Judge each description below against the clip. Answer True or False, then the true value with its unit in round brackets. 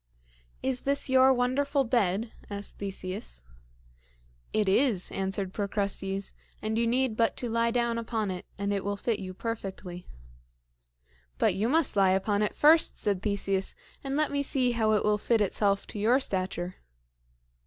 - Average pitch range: True (3.9 semitones)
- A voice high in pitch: True (215 Hz)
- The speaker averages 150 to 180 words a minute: True (160 wpm)